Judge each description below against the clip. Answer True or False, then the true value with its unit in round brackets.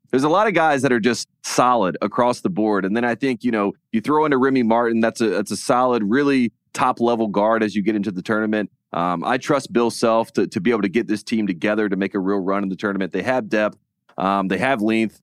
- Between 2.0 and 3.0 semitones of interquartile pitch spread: True (2.6 semitones)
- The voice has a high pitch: False (110 Hz)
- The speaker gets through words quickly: True (265 wpm)